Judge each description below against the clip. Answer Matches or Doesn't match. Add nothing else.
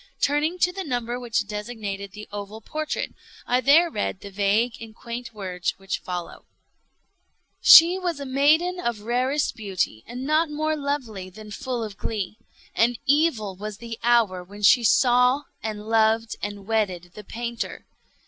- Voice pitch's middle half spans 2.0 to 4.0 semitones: Doesn't match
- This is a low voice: Doesn't match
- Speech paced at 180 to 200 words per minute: Doesn't match